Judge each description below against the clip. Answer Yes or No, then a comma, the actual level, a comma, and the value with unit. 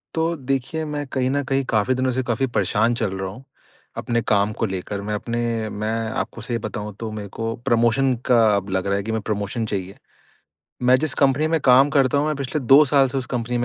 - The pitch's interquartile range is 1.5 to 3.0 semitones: No, average, 4.2 semitones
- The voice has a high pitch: No, low, 120 Hz